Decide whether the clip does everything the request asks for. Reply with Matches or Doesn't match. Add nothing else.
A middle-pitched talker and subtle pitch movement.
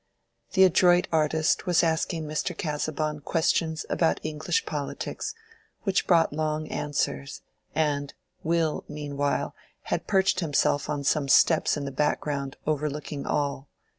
Matches